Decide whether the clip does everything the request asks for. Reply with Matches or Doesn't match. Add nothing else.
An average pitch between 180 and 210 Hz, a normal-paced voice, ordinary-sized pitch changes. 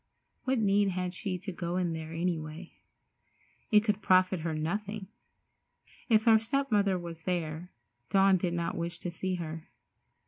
Matches